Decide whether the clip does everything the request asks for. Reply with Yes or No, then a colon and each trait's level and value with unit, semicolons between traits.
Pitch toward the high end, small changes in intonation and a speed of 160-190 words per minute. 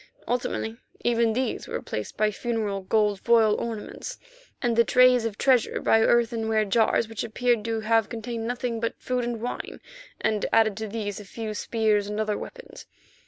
Yes: high, 225 Hz; narrow, 1.7 semitones; average, 170 wpm